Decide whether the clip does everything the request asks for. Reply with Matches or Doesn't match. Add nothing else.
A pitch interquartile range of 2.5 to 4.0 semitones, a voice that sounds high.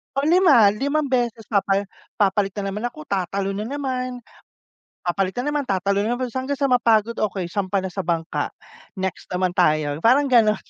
Doesn't match